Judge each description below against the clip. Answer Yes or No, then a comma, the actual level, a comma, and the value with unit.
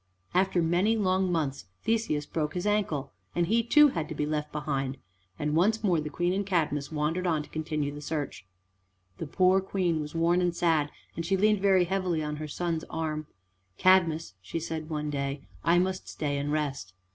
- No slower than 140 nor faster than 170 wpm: No, average, 190 wpm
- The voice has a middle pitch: Yes, medium, 165 Hz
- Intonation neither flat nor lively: Yes, average, 3.7 semitones